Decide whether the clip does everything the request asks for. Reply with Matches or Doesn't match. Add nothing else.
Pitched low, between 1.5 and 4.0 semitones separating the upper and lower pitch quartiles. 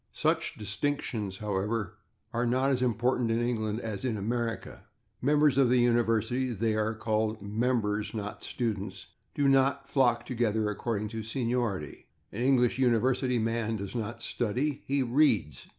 Matches